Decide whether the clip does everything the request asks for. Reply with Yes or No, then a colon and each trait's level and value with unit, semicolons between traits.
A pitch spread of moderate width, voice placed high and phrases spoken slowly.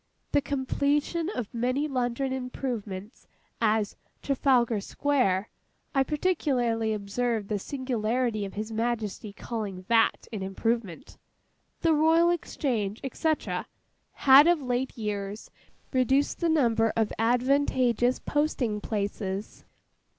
Yes: average, 4.5 semitones; high, 240 Hz; slow, 105 wpm